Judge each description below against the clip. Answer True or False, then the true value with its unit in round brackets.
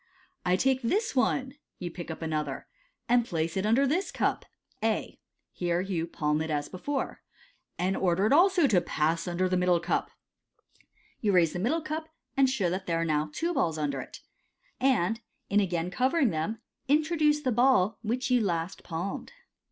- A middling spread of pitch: False (7.7 semitones)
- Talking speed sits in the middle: True (190 wpm)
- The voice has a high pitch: True (195 Hz)